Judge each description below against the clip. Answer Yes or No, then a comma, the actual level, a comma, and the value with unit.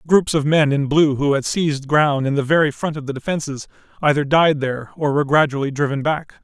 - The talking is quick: Yes, fast, 225 wpm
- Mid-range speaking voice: Yes, medium, 145 Hz